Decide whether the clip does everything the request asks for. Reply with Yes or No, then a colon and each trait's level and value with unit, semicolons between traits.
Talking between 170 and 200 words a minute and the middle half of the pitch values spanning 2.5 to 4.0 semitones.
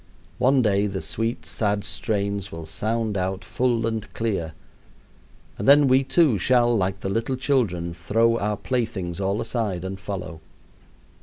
No: average, 150 wpm; average, 3.5 semitones